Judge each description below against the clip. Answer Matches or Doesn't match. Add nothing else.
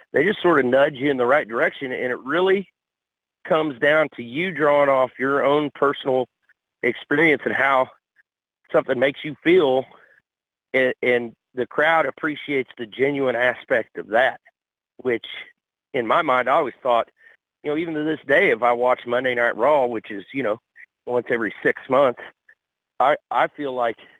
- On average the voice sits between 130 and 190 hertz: Matches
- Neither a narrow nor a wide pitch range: Matches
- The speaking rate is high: Doesn't match